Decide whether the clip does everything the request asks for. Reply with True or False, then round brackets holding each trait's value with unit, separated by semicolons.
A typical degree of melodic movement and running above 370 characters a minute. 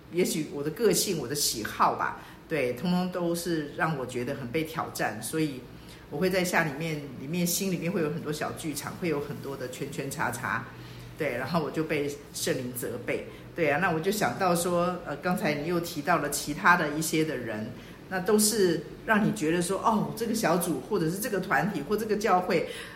False (3.7 semitones; 290 characters per minute)